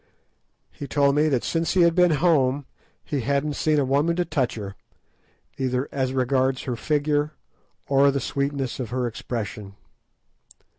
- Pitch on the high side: No, medium, 140 Hz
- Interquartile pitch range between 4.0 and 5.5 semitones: No, average, 2.7 semitones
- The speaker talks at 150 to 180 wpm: Yes, average, 155 wpm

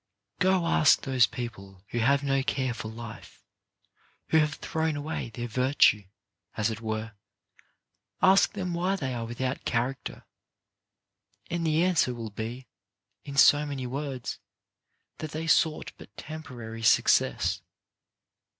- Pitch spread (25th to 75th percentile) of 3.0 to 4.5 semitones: No, average, 5.1 semitones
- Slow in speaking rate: Yes, slow, 130 wpm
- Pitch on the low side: Yes, low, 130 Hz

